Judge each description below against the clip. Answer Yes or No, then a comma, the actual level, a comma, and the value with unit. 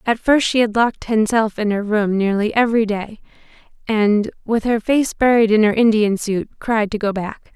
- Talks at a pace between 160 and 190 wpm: No, fast, 205 wpm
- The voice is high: Yes, high, 220 Hz